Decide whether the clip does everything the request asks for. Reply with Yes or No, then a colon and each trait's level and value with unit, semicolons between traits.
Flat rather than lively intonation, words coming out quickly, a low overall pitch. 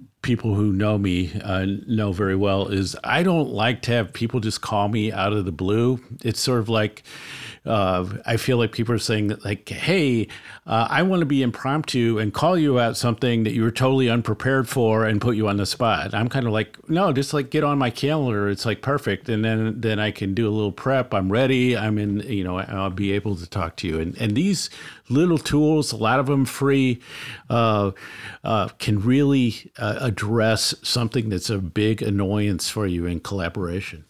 No: average, 3.9 semitones; fast, 210 wpm; low, 110 Hz